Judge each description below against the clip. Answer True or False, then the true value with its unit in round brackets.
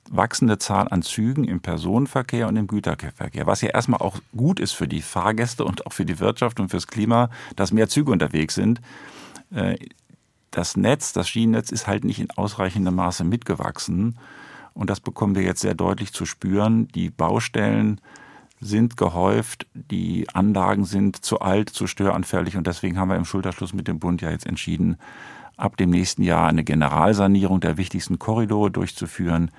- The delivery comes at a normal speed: True (170 wpm)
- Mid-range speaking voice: False (100 Hz)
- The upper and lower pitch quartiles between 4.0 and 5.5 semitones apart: False (3.6 semitones)